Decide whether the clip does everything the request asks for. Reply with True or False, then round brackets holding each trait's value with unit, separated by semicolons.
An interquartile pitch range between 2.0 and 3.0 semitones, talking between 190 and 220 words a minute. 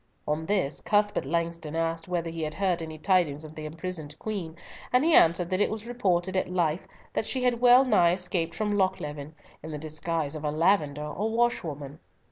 False (4.1 semitones; 195 wpm)